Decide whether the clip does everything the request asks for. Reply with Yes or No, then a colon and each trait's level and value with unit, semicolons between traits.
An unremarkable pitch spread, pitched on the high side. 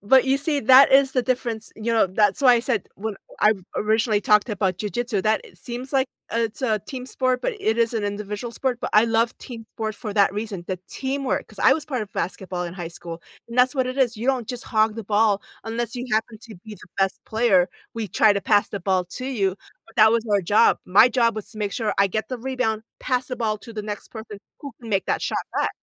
Yes: average, 3.2 semitones; high, 220 Hz